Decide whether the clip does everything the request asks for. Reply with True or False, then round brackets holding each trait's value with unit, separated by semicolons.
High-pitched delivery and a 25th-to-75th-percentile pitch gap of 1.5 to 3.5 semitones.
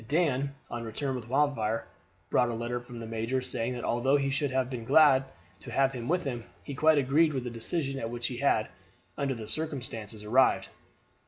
False (130 Hz; 3.0 semitones)